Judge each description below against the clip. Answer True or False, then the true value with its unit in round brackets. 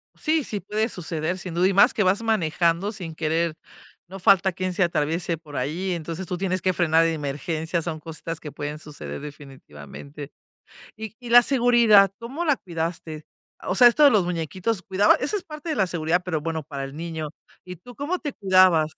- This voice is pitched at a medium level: True (175 Hz)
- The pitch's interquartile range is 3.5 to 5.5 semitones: True (4.3 semitones)